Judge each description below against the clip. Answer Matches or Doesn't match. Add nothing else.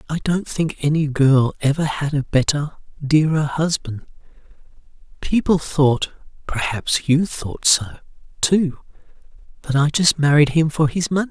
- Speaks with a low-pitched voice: Doesn't match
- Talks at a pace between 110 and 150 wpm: Matches